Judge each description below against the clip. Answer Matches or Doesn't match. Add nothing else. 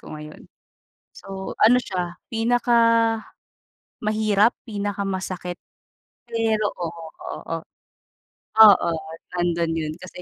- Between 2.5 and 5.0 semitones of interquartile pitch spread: Matches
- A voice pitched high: Matches